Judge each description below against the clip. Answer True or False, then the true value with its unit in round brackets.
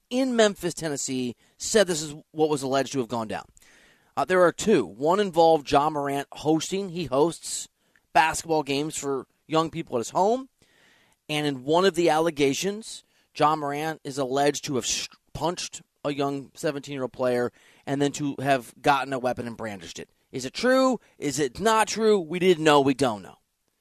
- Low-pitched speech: False (150 Hz)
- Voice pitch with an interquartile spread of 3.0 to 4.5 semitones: True (4.1 semitones)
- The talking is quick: False (185 wpm)